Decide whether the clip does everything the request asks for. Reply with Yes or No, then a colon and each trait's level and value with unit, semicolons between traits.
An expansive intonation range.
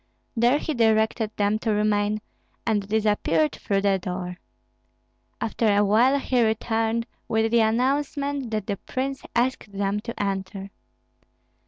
No: average, 2.7 semitones